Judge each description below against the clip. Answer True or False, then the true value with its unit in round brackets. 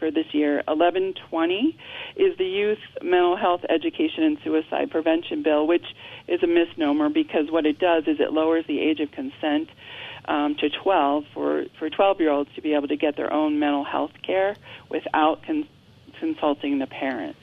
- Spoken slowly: False (180 wpm)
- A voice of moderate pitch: True (165 Hz)